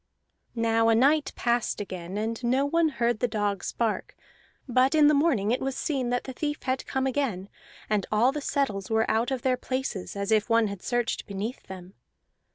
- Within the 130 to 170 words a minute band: No, average, 195 wpm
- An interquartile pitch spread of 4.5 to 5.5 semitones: No, average, 4.0 semitones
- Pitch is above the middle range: Yes, high, 240 Hz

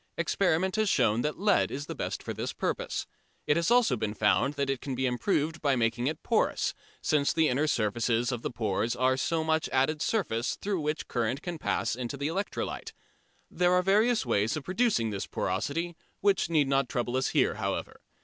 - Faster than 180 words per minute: Yes, average, 195 wpm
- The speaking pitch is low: No, medium, 145 Hz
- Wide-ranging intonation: Yes, wide, 5.9 semitones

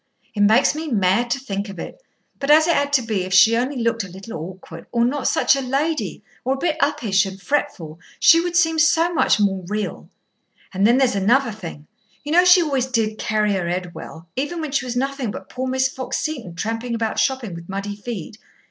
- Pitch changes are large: Yes, wide, 5.9 semitones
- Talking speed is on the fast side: Yes, fast, 220 wpm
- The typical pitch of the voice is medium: No, high, 235 Hz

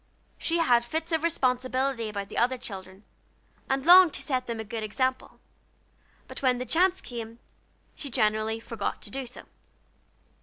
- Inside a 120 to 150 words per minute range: No, average, 160 wpm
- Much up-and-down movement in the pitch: No, average, 3.6 semitones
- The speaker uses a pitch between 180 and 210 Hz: No, very high, 250 Hz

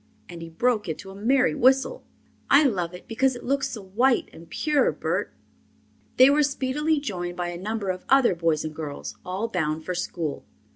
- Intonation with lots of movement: Yes, wide, 7.2 semitones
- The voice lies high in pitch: Yes, high, 205 Hz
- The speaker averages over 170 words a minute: Yes, average, 190 wpm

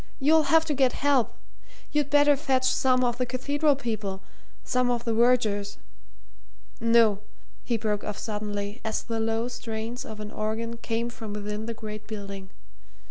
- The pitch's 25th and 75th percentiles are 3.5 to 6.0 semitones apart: No, average, 3.1 semitones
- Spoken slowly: No, average, 160 wpm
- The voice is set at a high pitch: Yes, high, 230 Hz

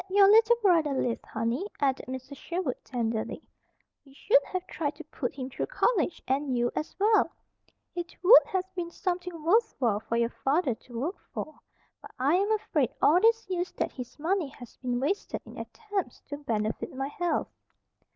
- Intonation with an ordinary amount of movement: No, wide, 6.5 semitones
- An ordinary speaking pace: Yes, average, 180 wpm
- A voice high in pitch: Yes, very high, 305 Hz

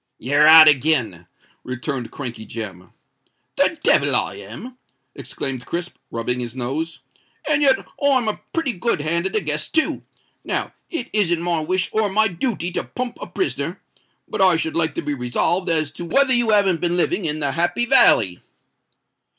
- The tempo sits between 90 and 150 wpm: No, average, 170 wpm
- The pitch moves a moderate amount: No, wide, 7.2 semitones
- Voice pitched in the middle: Yes, medium, 165 Hz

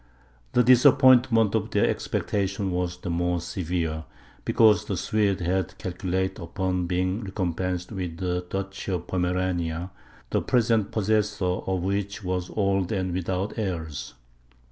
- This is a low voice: Yes, very low, 95 Hz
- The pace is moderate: No, slow, 130 wpm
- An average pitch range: No, narrow, 2.1 semitones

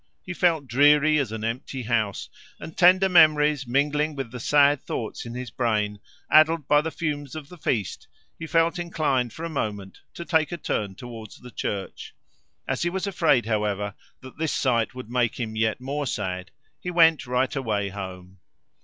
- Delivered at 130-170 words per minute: No, average, 180 wpm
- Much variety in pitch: Yes, wide, 5.9 semitones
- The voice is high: No, low, 130 Hz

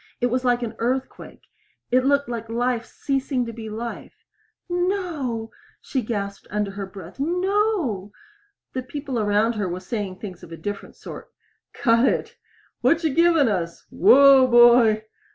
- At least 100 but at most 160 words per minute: Yes, average, 150 wpm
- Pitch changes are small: No, average, 4.6 semitones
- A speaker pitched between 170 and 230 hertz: No, high, 240 Hz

